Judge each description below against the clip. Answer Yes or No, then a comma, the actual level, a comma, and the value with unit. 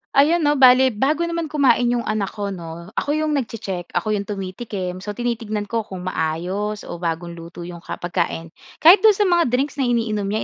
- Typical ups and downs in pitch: No, wide, 6.8 semitones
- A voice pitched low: No, high, 215 Hz